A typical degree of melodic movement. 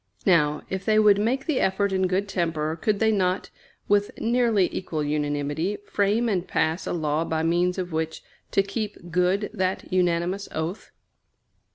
Yes: average, 3.9 semitones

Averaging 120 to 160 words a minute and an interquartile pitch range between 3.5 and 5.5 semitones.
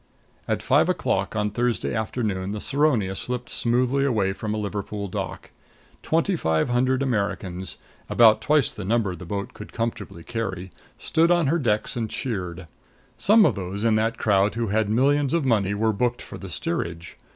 No: average, 175 wpm; average, 4.1 semitones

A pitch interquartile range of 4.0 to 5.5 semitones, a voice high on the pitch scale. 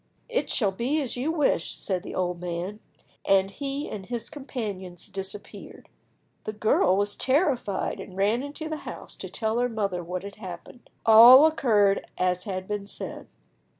Yes: average, 5.0 semitones; high, 210 Hz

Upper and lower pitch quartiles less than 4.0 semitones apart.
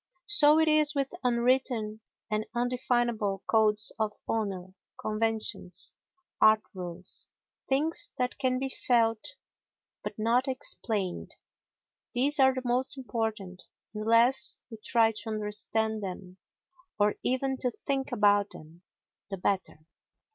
Yes: average, 3.6 semitones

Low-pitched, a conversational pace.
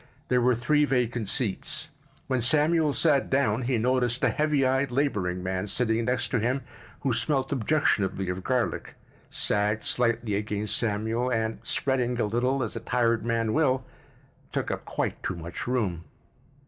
Yes: low, 120 Hz; average, 160 wpm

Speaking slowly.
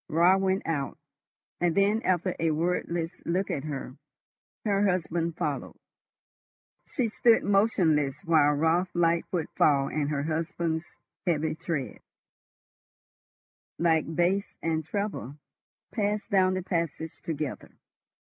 Yes: slow, 115 wpm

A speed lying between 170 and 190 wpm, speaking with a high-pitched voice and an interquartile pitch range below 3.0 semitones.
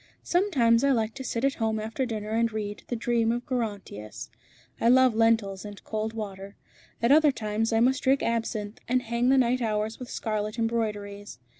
Yes: average, 185 wpm; high, 225 Hz; narrow, 2.4 semitones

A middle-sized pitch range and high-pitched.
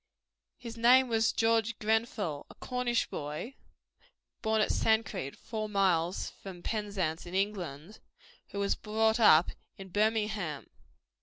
Yes: average, 3.7 semitones; high, 210 Hz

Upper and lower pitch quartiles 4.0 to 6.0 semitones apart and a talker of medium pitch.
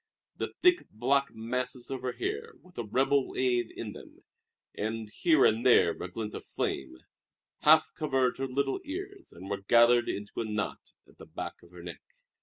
No: average, 4.6 semitones; low, 125 Hz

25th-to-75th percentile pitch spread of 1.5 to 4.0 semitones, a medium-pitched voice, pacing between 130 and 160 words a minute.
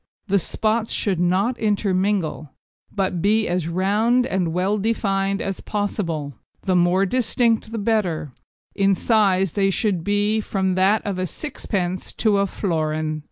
No: average, 2.8 semitones; high, 195 Hz; average, 145 wpm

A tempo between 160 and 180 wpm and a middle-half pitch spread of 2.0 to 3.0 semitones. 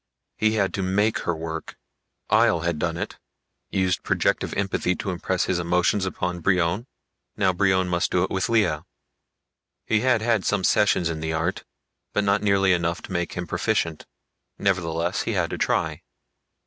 Yes: average, 170 wpm; narrow, 2.6 semitones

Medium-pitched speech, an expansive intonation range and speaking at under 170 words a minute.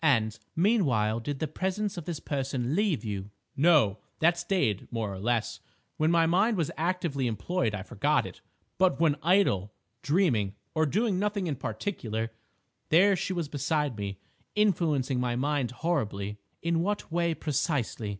Yes: medium, 150 Hz; wide, 7.3 semitones; average, 155 wpm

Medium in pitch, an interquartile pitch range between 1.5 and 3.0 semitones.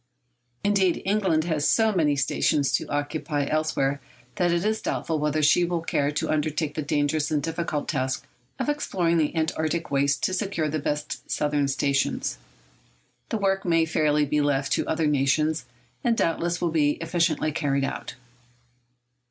Yes: medium, 155 Hz; average, 2.7 semitones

